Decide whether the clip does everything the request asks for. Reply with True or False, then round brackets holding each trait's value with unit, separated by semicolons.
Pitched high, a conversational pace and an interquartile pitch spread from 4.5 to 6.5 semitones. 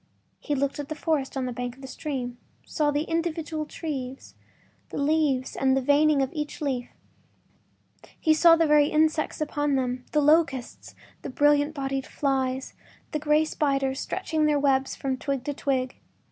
False (285 Hz; 165 wpm; 2.4 semitones)